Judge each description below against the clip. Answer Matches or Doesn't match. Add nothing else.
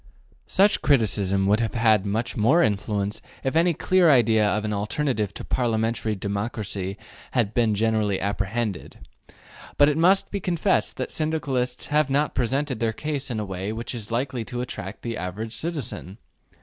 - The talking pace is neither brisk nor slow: Matches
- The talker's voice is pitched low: Matches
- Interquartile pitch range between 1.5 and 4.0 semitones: Doesn't match